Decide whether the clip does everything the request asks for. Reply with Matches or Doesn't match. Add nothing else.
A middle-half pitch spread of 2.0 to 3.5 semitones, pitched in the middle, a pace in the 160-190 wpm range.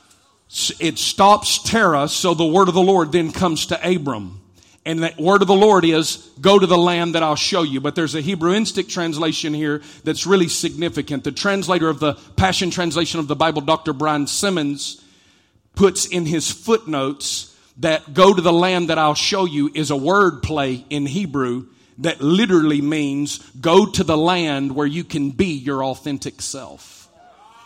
Doesn't match